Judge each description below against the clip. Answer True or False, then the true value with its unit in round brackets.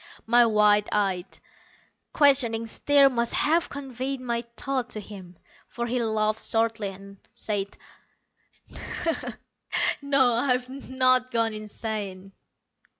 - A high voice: True (230 Hz)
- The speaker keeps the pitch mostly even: False (3.4 semitones)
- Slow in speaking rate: True (105 wpm)